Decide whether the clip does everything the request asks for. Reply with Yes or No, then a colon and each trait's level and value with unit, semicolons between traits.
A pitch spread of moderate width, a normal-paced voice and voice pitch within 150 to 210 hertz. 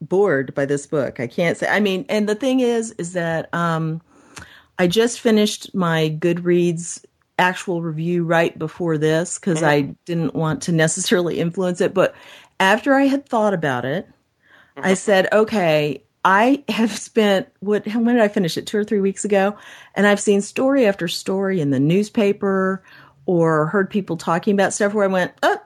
Yes: average, 4.3 semitones; average, 180 wpm; high, 190 Hz